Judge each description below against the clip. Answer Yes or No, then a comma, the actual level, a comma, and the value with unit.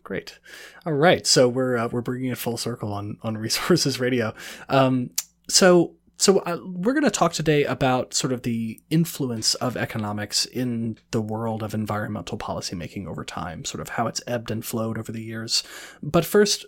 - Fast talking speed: No, average, 180 wpm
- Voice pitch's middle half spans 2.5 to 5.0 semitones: No, wide, 5.4 semitones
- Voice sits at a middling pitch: No, low, 125 Hz